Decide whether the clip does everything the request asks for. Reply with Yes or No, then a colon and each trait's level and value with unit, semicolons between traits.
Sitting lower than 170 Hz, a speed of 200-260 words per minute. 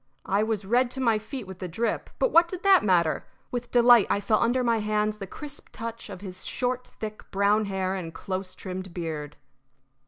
No: high, 215 Hz; fast, 205 wpm